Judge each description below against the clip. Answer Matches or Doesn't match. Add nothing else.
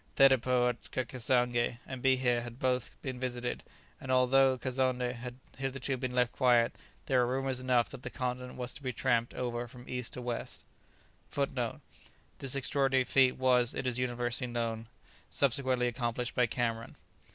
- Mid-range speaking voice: Doesn't match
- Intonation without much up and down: Matches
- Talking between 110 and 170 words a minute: Matches